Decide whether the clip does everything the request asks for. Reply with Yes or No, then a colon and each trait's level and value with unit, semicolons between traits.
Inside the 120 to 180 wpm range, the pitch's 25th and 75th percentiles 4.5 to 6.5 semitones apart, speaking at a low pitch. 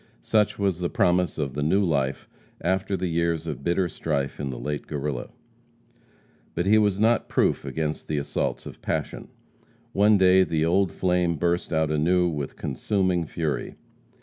No: average, 165 wpm; average, 3.8 semitones; very low, 85 Hz